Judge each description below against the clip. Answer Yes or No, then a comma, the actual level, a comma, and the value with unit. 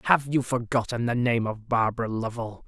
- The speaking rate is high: No, average, 180 wpm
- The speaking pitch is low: Yes, low, 120 Hz